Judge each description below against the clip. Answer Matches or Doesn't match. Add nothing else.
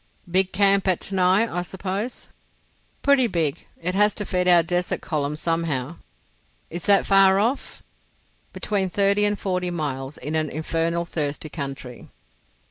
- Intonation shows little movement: Doesn't match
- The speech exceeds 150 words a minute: Doesn't match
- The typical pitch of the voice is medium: Matches